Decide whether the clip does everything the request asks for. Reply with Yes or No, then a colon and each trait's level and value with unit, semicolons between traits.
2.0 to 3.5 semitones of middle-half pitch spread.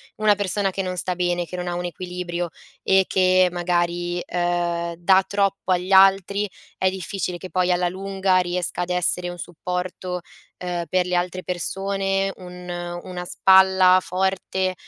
No: narrow, 1.3 semitones